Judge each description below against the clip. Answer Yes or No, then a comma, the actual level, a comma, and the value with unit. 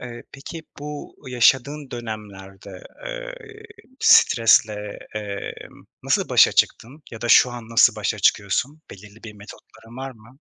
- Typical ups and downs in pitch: Yes, average, 4.5 semitones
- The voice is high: No, low, 120 Hz